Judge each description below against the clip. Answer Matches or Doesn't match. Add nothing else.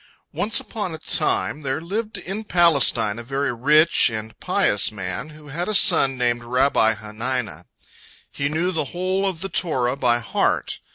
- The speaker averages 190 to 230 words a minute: Doesn't match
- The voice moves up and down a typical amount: Doesn't match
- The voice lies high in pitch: Doesn't match